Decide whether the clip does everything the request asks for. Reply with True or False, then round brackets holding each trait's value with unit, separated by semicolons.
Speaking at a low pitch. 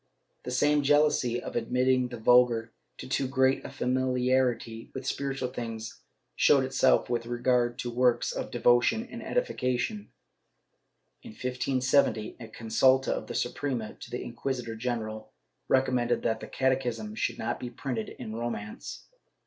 True (125 Hz)